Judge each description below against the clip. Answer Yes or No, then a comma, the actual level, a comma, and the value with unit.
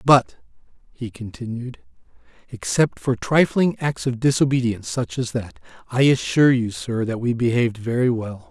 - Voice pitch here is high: No, low, 125 Hz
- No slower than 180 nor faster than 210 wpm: No, average, 150 wpm